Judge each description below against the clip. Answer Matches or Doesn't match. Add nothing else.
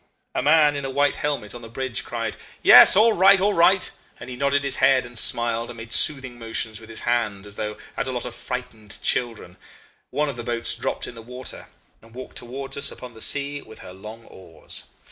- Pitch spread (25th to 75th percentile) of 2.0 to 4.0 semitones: Matches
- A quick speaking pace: Matches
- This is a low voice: Matches